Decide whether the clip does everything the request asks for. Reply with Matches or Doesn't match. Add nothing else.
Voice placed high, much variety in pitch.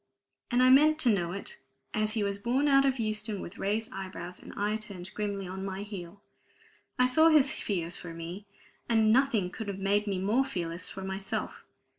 Doesn't match